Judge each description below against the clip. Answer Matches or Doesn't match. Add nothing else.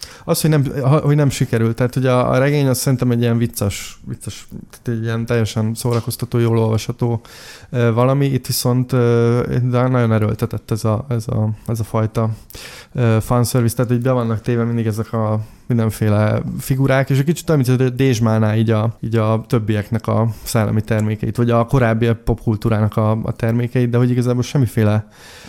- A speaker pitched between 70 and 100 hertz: Doesn't match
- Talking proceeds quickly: Matches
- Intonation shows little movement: Matches